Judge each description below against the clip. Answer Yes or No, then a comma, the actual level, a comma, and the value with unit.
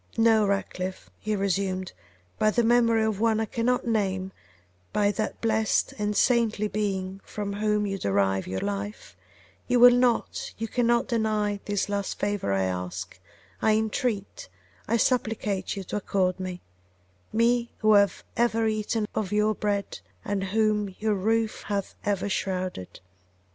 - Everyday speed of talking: Yes, average, 150 wpm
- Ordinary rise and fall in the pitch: No, narrow, 2.3 semitones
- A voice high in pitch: Yes, high, 210 Hz